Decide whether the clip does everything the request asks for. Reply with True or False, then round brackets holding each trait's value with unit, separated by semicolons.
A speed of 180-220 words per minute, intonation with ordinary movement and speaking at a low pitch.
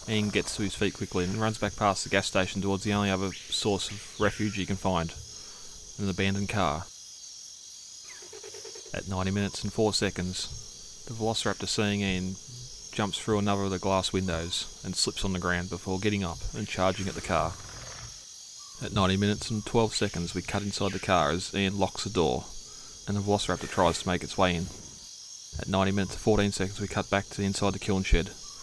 False (200 wpm; 1.9 semitones; 100 Hz)